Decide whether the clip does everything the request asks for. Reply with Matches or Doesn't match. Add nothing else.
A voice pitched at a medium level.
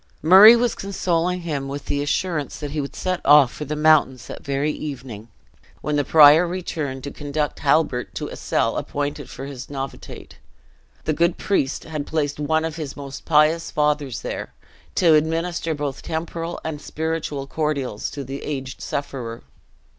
Matches